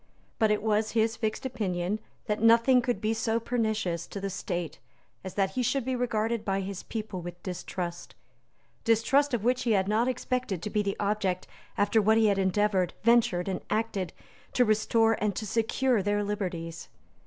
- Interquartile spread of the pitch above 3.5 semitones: No, average, 2.9 semitones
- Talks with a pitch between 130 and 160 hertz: No, high, 215 Hz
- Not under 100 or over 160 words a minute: No, average, 180 wpm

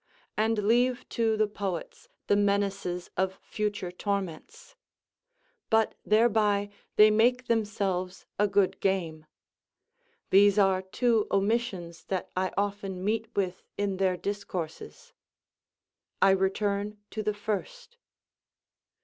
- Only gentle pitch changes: Yes, narrow, 2.2 semitones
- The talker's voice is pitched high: Yes, high, 205 Hz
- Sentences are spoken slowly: Yes, slow, 110 wpm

